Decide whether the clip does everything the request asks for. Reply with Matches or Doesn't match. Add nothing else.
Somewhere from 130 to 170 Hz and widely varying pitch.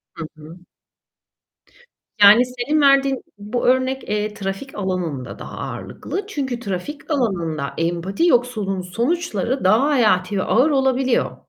Doesn't match